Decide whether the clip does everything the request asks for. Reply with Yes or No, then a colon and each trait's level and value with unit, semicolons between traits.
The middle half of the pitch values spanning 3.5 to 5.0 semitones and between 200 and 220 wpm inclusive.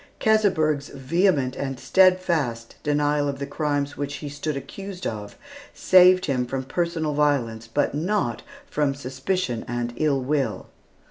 No: average, 4.1 semitones; slow, 135 wpm